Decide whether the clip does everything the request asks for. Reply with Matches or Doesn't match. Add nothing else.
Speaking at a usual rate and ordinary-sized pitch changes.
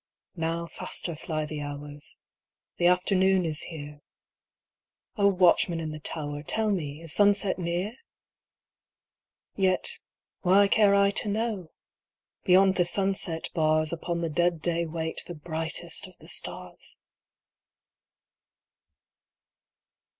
Doesn't match